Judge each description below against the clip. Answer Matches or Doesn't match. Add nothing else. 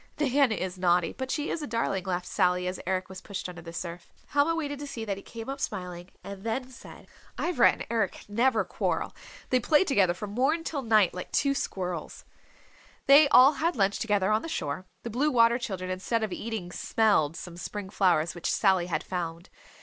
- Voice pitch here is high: Matches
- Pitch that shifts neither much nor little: Doesn't match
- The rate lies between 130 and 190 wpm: Doesn't match